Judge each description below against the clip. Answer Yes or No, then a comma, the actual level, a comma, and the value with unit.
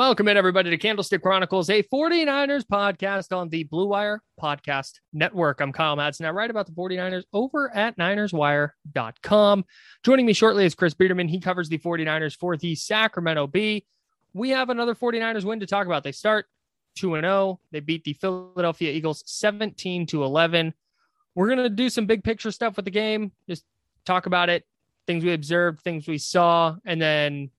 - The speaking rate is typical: Yes, average, 175 wpm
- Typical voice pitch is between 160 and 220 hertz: Yes, medium, 185 Hz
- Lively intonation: No, average, 4.4 semitones